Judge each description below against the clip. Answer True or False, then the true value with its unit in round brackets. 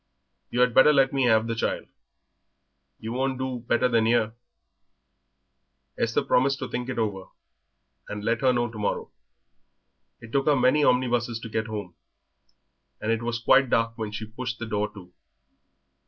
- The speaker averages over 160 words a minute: True (170 wpm)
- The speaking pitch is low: True (120 Hz)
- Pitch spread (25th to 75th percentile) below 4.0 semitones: True (2.5 semitones)